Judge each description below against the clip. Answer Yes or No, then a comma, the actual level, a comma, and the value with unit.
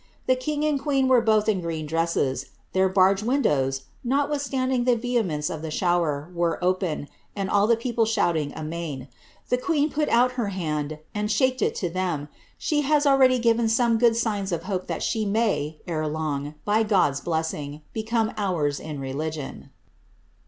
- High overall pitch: Yes, high, 195 Hz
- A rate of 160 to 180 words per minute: Yes, average, 170 wpm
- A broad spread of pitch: Yes, wide, 7.3 semitones